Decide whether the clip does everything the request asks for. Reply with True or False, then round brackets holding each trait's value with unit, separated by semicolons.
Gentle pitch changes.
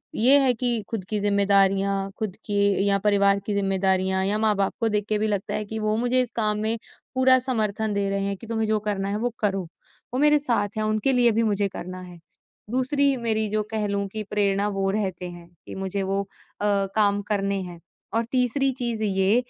True (2.2 semitones)